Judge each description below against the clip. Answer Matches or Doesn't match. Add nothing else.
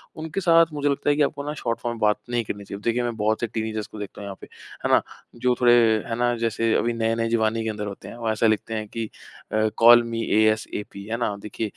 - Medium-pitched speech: Doesn't match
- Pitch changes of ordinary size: Doesn't match